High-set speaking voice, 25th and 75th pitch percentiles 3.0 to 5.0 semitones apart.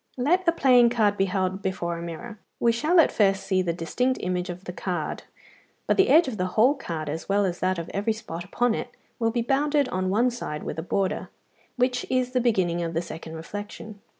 No: high, 205 Hz; wide, 5.6 semitones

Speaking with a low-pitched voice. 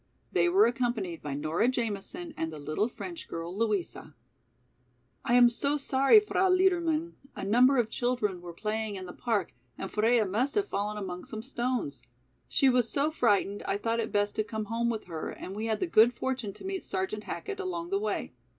No: high, 230 Hz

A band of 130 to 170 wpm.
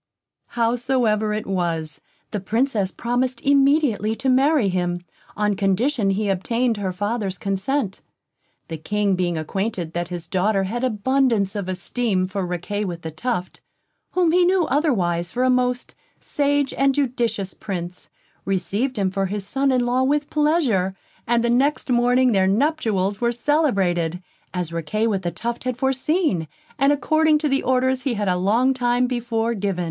Yes: average, 160 wpm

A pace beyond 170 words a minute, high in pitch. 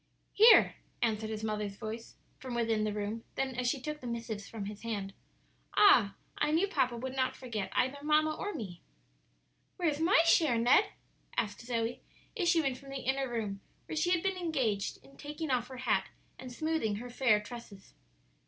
Yes: average, 180 wpm; high, 245 Hz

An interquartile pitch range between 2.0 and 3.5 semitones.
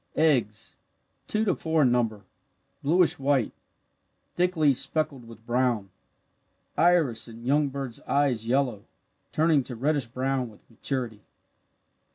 No: average, 4.6 semitones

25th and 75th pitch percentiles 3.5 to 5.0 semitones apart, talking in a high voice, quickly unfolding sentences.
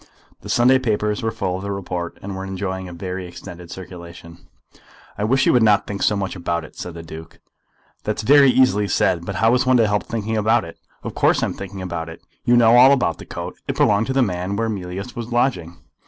No: average, 4.2 semitones; low, 100 Hz; fast, 235 wpm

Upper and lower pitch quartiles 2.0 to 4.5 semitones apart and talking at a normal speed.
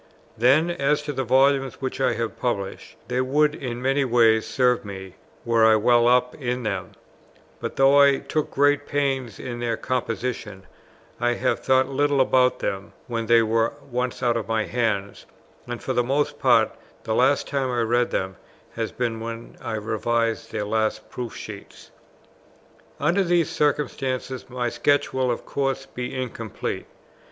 Yes: average, 2.9 semitones; average, 165 wpm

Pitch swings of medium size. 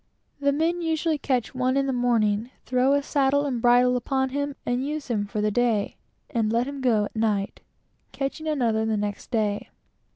Yes: average, 4.1 semitones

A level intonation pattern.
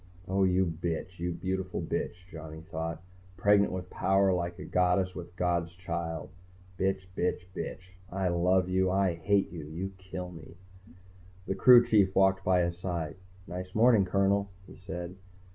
Yes: narrow, 1.7 semitones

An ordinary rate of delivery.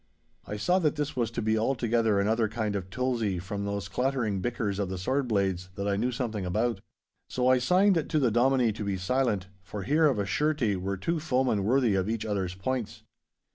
No: fast, 210 wpm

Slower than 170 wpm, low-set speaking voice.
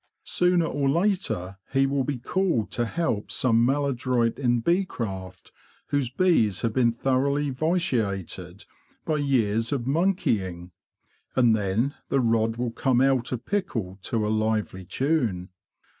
Yes: average, 145 wpm; low, 120 Hz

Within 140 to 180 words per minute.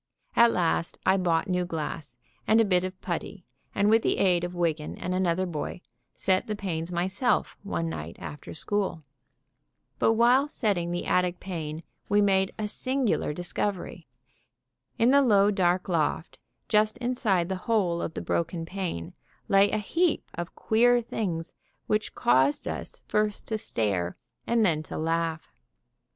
Yes: average, 155 wpm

